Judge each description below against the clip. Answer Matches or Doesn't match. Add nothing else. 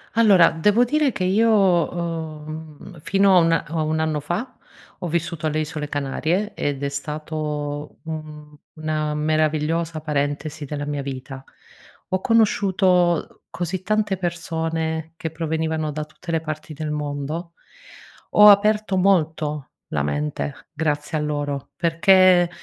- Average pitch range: Matches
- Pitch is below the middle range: Doesn't match